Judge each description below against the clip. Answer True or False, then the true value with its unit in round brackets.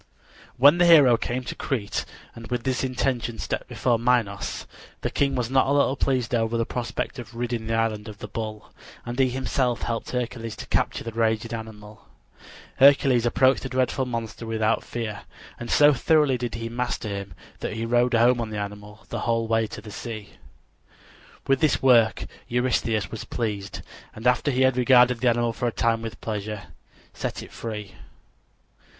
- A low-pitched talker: True (115 Hz)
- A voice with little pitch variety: True (2.2 semitones)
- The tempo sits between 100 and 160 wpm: False (180 wpm)